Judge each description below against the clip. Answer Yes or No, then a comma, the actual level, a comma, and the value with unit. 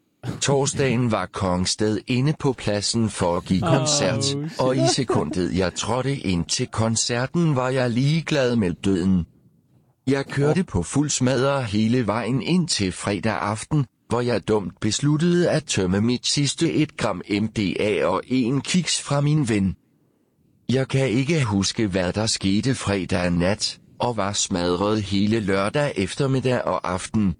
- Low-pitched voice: Yes, low, 120 Hz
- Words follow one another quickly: No, average, 150 wpm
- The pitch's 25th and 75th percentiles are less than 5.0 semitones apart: No, wide, 5.5 semitones